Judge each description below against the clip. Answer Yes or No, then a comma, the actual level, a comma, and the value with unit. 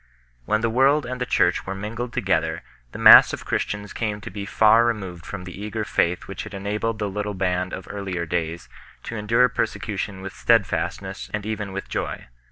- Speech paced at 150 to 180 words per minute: No, average, 190 wpm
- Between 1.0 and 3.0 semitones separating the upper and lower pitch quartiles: Yes, average, 2.7 semitones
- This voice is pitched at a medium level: No, low, 105 Hz